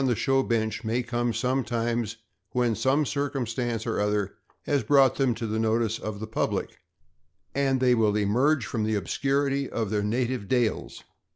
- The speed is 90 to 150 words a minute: No, average, 170 wpm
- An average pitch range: Yes, average, 3.2 semitones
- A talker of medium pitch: No, low, 120 Hz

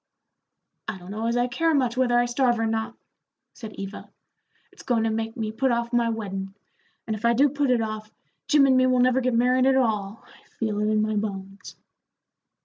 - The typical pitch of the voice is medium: No, high, 230 Hz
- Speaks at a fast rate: Yes, fast, 215 wpm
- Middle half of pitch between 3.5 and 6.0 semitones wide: No, average, 2.8 semitones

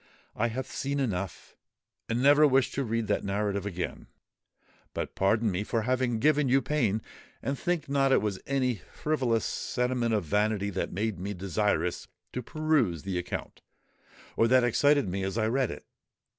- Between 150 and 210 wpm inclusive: Yes, average, 165 wpm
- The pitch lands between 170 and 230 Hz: No, low, 115 Hz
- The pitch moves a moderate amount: Yes, average, 5.0 semitones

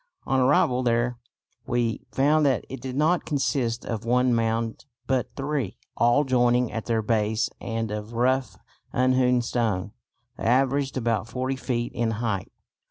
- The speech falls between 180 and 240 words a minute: No, average, 150 wpm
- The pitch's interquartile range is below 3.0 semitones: Yes, narrow, 2.4 semitones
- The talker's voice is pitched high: No, low, 120 Hz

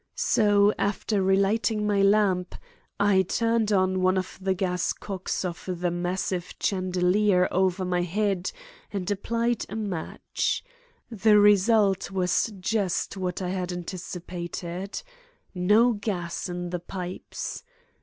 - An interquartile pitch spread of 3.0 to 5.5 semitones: No, narrow, 2.4 semitones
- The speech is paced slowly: Yes, slow, 120 wpm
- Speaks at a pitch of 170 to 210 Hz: Yes, high, 190 Hz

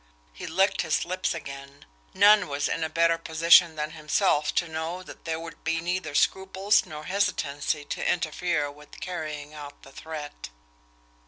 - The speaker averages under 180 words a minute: Yes, average, 160 wpm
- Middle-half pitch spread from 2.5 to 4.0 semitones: Yes, average, 3.1 semitones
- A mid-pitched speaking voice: Yes, medium, 160 Hz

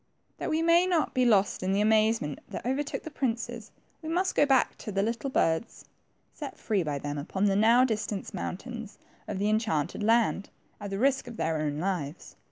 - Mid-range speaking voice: No, high, 220 Hz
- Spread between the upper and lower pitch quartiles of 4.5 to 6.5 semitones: Yes, average, 4.9 semitones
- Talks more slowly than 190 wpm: No, average, 200 wpm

